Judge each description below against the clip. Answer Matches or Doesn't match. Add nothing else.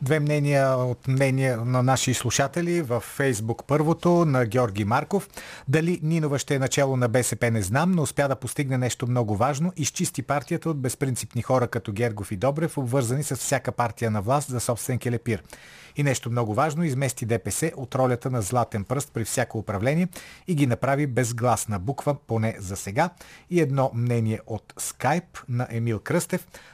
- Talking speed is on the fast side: Matches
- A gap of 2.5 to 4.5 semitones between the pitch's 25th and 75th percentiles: Matches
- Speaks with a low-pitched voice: Matches